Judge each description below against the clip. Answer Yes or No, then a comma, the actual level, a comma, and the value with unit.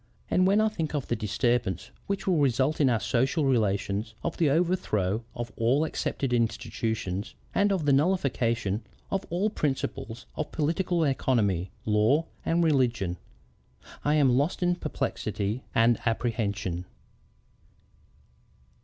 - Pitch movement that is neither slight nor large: No, wide, 6.1 semitones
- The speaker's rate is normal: No, slow, 130 wpm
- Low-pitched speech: Yes, low, 130 Hz